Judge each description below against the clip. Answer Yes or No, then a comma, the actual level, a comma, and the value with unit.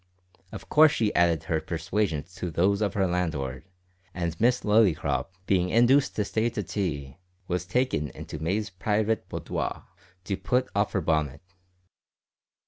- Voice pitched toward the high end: No, very low, 95 Hz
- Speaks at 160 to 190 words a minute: No, average, 145 wpm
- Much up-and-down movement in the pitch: No, average, 4.6 semitones